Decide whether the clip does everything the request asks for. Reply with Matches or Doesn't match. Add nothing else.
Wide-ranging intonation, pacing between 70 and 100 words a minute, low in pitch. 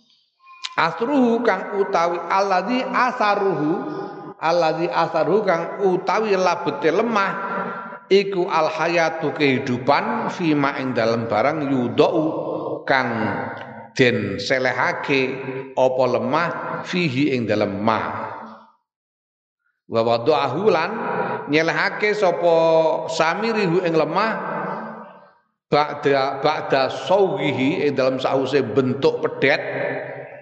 Doesn't match